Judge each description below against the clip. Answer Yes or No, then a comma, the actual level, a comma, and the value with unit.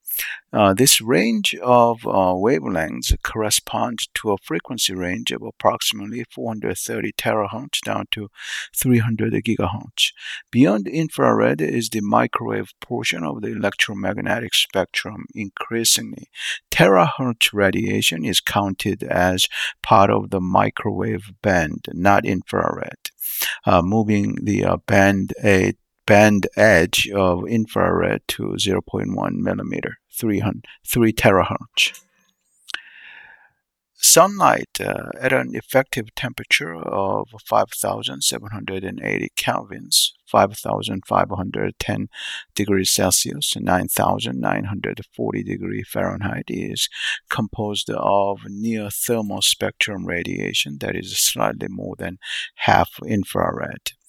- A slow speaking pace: Yes, slow, 95 wpm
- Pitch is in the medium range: No, low, 100 Hz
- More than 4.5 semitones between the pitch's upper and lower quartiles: No, average, 3.1 semitones